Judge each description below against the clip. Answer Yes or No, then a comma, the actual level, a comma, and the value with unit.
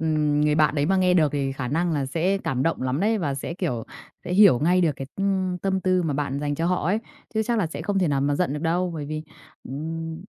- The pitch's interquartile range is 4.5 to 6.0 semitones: No, average, 4.0 semitones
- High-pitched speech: No, medium, 160 Hz